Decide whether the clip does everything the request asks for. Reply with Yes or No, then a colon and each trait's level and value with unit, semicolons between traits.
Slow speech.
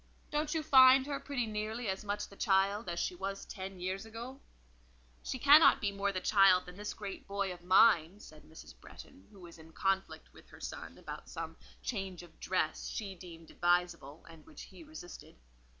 No: average, 190 wpm